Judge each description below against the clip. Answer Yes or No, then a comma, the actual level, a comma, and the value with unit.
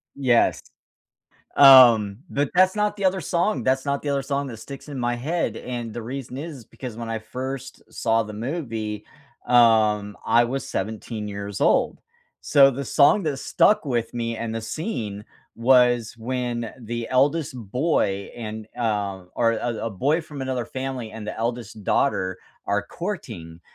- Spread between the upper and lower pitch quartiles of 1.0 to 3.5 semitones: No, average, 3.9 semitones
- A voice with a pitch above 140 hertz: No, low, 120 Hz